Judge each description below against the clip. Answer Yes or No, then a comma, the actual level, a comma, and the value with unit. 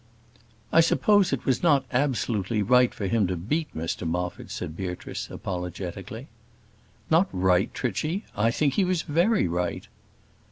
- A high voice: No, low, 115 Hz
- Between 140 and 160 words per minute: Yes, average, 145 wpm